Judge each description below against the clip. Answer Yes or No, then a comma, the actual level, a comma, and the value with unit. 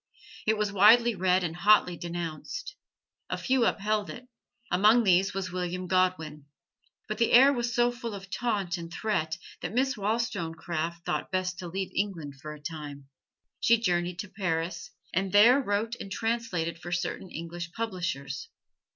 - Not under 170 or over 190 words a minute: No, average, 160 wpm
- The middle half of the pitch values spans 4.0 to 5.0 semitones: Yes, average, 4.3 semitones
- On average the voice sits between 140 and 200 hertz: Yes, medium, 185 Hz